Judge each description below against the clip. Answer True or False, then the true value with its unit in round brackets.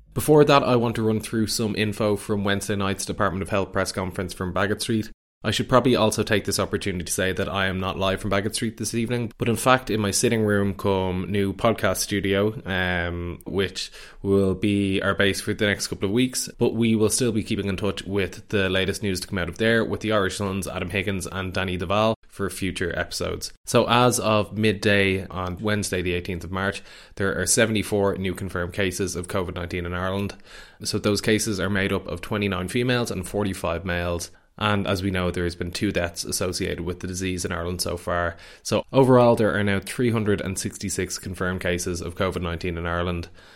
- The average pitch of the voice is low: True (100 Hz)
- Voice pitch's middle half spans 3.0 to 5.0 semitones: False (2.6 semitones)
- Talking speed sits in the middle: False (210 wpm)